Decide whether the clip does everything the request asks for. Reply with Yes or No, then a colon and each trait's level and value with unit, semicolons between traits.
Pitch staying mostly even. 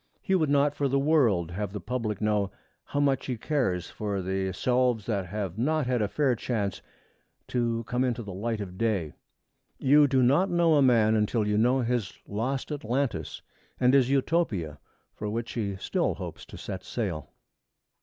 No: average, 4.8 semitones